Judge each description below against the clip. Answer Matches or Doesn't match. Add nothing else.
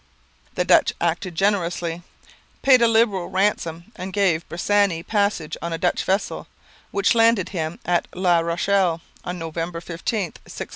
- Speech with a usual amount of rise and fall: Matches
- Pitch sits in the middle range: Matches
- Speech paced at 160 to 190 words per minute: Doesn't match